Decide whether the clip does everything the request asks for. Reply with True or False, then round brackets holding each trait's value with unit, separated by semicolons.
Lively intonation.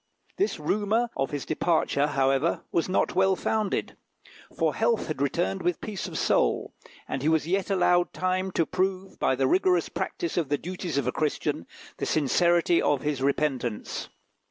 False (4.7 semitones)